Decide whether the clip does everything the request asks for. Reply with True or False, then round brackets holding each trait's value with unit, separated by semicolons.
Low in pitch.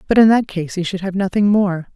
False (190 Hz)